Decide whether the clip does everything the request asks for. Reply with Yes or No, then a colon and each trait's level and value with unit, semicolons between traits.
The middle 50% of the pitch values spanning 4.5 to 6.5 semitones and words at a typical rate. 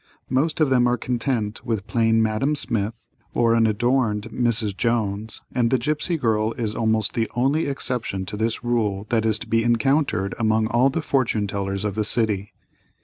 No: narrow, 2.5 semitones; average, 175 wpm